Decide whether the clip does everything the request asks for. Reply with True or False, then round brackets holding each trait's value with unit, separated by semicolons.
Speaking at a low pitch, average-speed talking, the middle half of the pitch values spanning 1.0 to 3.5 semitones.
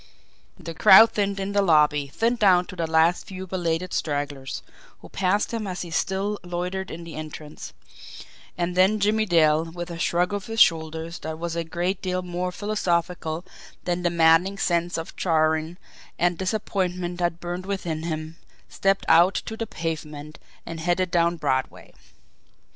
False (175 Hz; 165 wpm; 2.6 semitones)